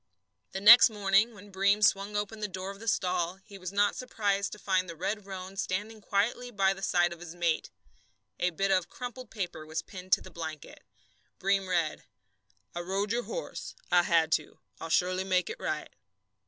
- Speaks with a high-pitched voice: Yes, high, 195 Hz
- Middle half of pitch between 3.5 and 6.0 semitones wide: No, narrow, 2.5 semitones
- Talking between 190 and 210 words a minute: Yes, average, 195 wpm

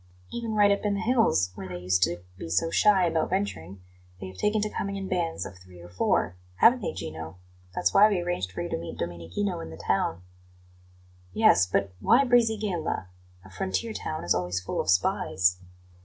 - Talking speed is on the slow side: No, average, 200 wpm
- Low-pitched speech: Yes, very low, 95 Hz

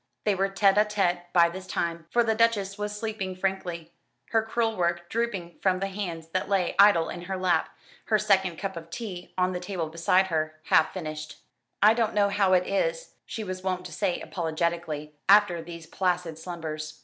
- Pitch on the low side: No, medium, 185 Hz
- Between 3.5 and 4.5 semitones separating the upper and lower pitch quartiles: No, average, 3.1 semitones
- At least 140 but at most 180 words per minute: No, average, 195 wpm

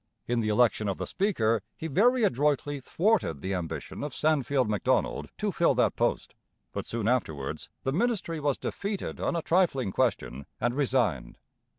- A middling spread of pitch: No, wide, 7.3 semitones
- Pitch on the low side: Yes, low, 130 Hz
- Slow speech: No, average, 165 wpm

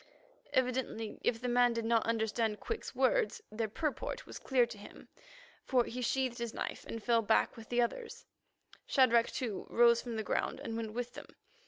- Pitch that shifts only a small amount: Yes, narrow, 1.8 semitones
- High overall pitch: Yes, high, 235 Hz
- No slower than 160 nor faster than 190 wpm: Yes, average, 185 wpm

